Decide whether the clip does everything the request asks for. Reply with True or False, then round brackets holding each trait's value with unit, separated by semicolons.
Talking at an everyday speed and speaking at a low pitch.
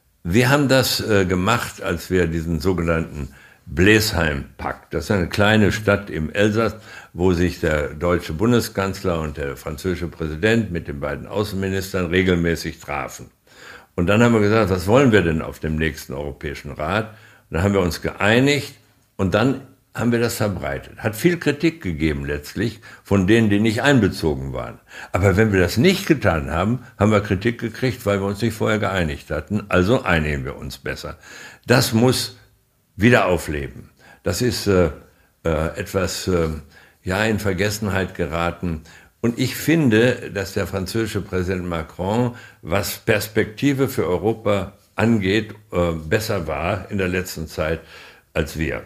True (155 wpm; 100 Hz)